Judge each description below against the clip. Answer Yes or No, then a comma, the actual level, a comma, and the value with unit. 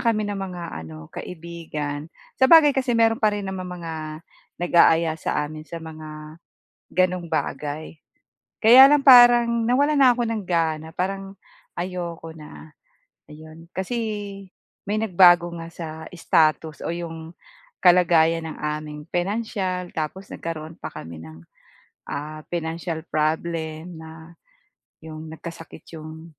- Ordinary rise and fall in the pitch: Yes, average, 3.6 semitones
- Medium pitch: Yes, medium, 170 Hz